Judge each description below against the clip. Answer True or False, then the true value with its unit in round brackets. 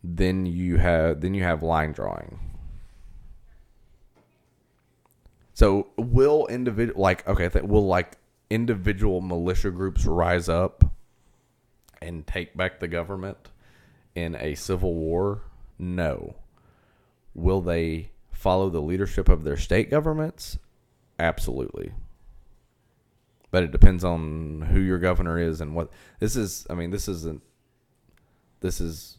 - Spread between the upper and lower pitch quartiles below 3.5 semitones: True (2.9 semitones)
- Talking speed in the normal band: False (120 wpm)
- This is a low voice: True (90 Hz)